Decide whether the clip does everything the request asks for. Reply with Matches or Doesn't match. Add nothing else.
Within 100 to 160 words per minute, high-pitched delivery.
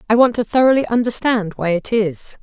Doesn't match